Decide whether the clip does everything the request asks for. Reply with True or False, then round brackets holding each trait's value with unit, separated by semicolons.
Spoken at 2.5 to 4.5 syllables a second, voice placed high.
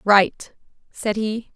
True (3.6 syllables/s; 210 Hz)